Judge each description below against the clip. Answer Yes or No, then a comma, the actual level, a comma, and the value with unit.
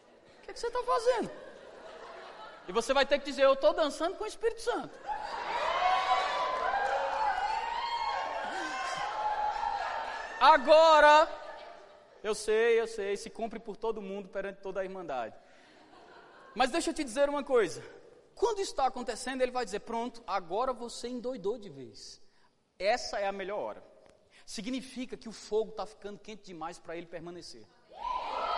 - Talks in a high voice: Yes, very high, 280 Hz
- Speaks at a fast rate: No, average, 140 wpm